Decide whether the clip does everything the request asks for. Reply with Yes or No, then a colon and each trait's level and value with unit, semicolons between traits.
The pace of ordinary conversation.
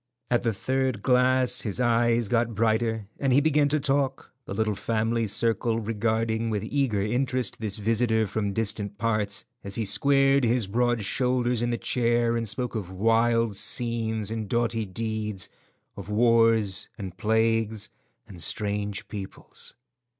Yes: average, 150 wpm